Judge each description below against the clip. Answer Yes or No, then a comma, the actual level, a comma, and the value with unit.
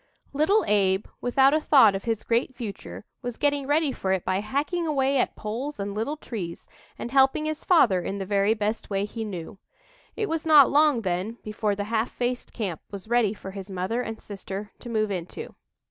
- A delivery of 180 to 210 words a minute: Yes, average, 200 wpm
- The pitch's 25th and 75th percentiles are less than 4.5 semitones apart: No, wide, 5.5 semitones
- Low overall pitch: No, high, 225 Hz